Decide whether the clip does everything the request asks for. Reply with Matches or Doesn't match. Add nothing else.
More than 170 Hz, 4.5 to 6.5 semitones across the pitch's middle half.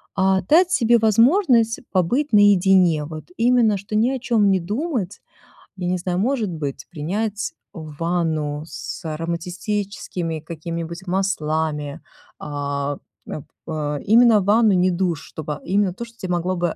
Matches